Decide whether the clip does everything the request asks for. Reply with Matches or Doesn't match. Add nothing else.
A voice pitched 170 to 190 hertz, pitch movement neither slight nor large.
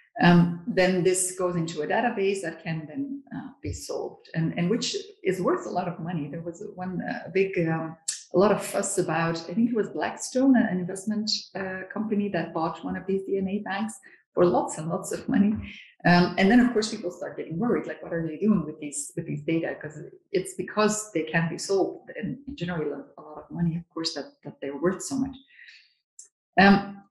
Matches